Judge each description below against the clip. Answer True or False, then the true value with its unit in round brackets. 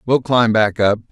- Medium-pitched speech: False (110 Hz)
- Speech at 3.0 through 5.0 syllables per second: True (4.6 syllables/s)